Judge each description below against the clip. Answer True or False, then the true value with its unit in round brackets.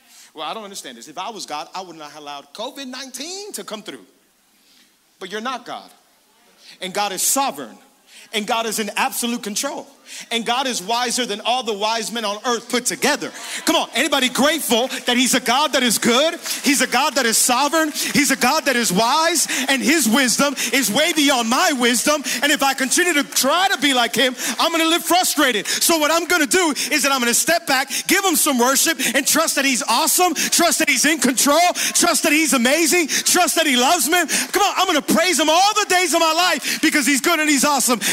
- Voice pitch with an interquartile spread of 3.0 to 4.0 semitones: False (4.8 semitones)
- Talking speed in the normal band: False (225 wpm)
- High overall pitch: True (275 Hz)